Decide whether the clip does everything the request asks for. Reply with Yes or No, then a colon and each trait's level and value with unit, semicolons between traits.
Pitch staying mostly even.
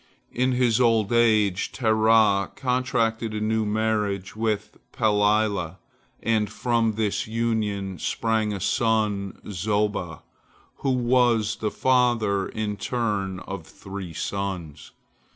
Yes: narrow, 2.3 semitones